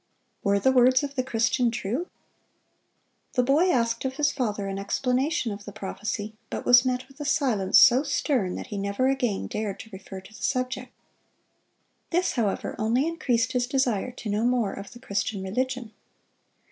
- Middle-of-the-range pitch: No, high, 245 Hz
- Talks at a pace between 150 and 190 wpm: Yes, average, 175 wpm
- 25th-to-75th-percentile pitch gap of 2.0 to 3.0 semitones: No, average, 4.0 semitones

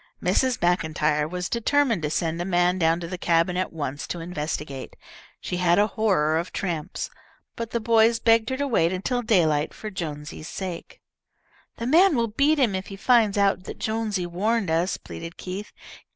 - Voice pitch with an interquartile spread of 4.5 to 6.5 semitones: Yes, average, 5.2 semitones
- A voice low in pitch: No, medium, 185 Hz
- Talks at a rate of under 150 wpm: No, average, 180 wpm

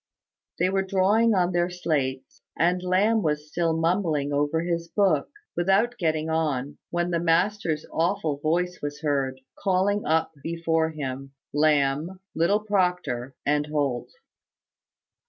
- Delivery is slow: Yes, slow, 130 wpm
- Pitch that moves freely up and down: No, average, 3.7 semitones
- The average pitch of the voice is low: No, medium, 165 Hz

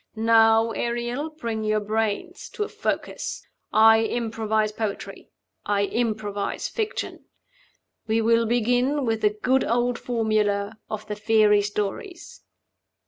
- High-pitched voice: Yes, high, 225 Hz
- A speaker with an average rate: No, slow, 120 wpm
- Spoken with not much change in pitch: Yes, narrow, 2.0 semitones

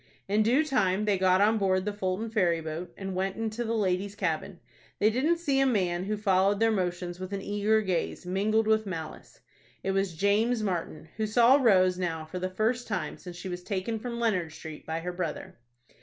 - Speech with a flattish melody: No, average, 3.2 semitones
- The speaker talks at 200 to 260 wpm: Yes, fast, 205 wpm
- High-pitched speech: Yes, high, 195 Hz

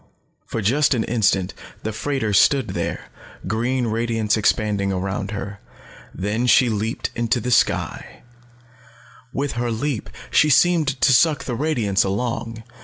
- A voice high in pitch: No, low, 115 Hz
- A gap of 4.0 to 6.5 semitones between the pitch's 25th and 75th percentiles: No, average, 3.6 semitones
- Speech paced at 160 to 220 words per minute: No, slow, 135 wpm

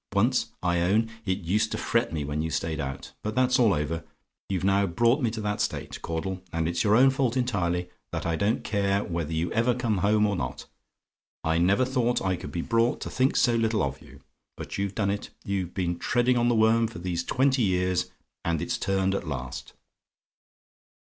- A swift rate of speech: Yes, fast, 210 wpm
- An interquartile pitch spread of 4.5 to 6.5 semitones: Yes, average, 5.1 semitones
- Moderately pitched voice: No, low, 100 Hz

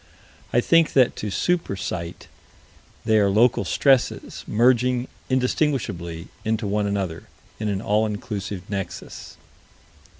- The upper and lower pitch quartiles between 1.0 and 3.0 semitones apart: No, average, 4.1 semitones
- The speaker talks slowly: Yes, slow, 120 wpm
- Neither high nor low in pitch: No, low, 105 Hz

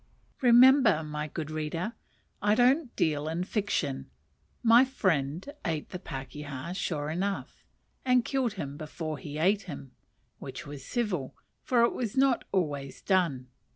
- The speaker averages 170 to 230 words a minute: No, average, 140 wpm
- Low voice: No, medium, 175 Hz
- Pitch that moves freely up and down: Yes, wide, 7.7 semitones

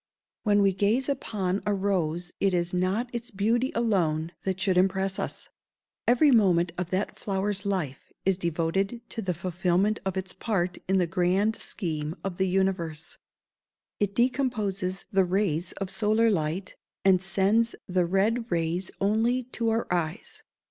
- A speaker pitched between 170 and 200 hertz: Yes, high, 190 Hz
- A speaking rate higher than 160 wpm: No, average, 155 wpm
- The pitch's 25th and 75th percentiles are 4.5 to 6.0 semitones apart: No, average, 3.0 semitones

